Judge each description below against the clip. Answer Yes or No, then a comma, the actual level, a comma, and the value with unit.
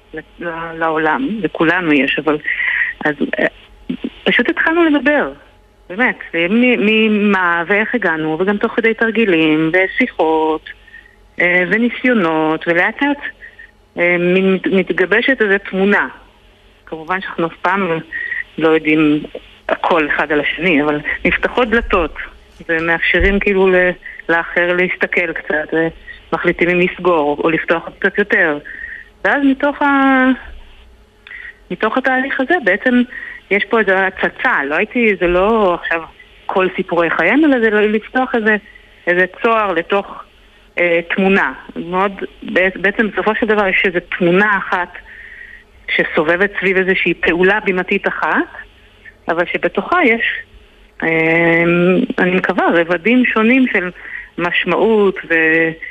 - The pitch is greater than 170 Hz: Yes, high, 190 Hz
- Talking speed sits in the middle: Yes, average, 110 wpm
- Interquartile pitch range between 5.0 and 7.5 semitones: Yes, wide, 5.6 semitones